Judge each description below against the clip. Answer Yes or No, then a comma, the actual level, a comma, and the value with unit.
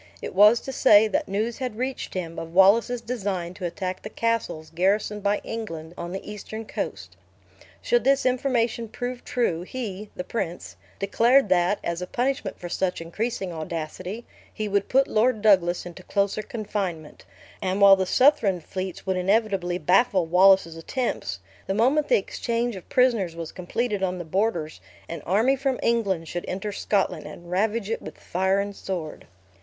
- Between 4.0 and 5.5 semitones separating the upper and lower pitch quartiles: Yes, average, 4.3 semitones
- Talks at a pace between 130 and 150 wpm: No, average, 170 wpm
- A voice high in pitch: Yes, high, 200 Hz